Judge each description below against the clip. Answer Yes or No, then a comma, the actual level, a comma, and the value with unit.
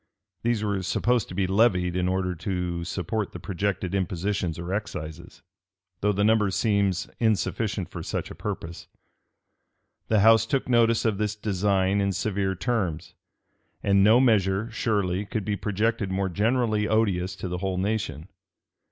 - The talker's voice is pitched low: Yes, low, 100 Hz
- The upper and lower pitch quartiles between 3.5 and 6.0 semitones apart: No, average, 2.9 semitones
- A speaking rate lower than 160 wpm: Yes, average, 150 wpm